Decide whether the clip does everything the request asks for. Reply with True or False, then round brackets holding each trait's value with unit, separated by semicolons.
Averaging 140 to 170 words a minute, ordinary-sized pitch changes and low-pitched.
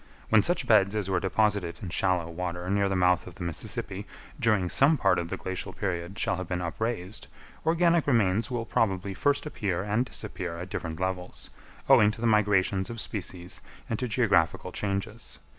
False (180 wpm; 3.3 semitones; 95 Hz)